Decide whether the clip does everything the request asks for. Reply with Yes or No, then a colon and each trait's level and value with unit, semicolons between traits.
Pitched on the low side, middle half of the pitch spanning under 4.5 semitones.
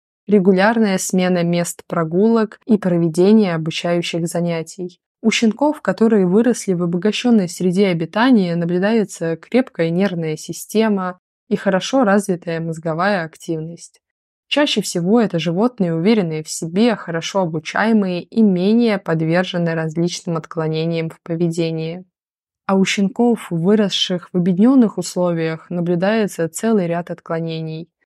No: medium, 180 Hz; average, 3.8 semitones